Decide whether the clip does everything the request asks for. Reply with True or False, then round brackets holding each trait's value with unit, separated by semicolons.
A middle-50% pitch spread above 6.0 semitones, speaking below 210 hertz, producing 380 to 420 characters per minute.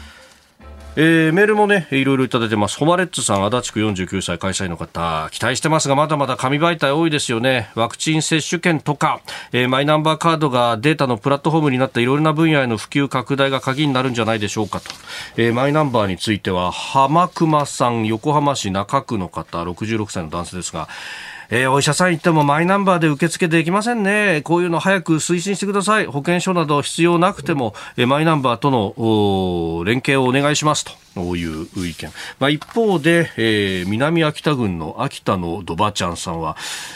True (7.2 semitones; 135 Hz; 410 characters per minute)